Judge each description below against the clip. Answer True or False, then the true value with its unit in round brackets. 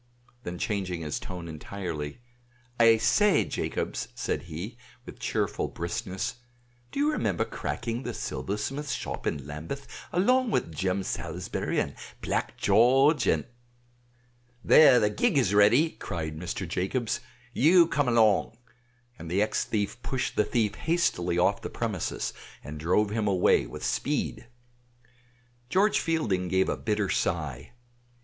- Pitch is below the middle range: True (105 Hz)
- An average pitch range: False (6.0 semitones)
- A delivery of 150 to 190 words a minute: False (140 wpm)